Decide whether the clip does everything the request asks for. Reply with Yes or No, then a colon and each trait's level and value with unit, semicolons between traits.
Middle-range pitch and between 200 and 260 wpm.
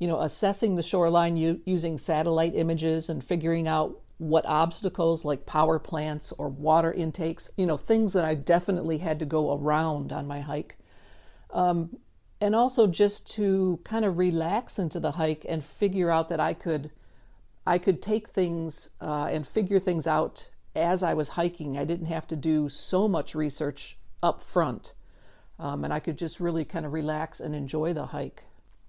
No: medium, 165 Hz; average, 180 wpm